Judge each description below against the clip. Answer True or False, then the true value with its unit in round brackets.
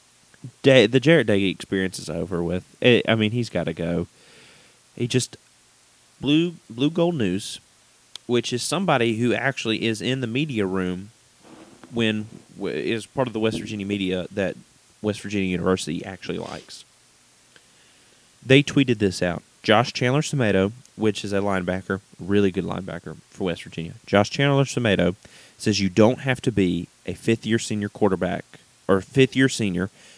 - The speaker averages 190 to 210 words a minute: False (165 wpm)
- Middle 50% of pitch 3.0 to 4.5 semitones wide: False (5.1 semitones)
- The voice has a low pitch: True (110 Hz)